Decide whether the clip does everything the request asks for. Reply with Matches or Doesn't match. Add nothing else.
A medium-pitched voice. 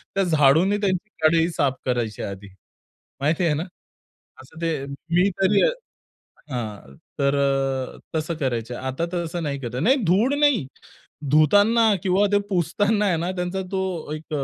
Matches